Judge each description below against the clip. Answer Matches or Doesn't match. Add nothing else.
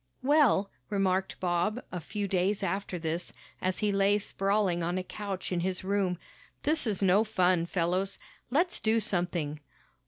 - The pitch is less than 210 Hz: Matches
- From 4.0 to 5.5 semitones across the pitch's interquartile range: Doesn't match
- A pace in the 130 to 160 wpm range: Matches